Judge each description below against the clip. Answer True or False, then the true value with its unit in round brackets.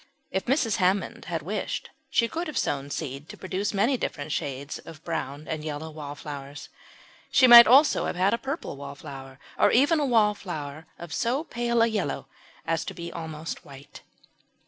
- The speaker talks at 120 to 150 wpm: False (170 wpm)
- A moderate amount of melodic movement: False (8.0 semitones)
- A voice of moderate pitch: True (170 Hz)